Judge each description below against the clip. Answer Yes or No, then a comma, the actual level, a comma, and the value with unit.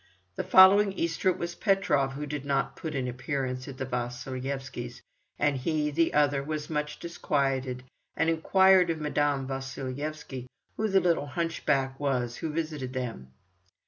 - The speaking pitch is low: No, medium, 145 Hz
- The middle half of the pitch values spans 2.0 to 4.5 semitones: Yes, average, 3.6 semitones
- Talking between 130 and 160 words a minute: Yes, average, 155 wpm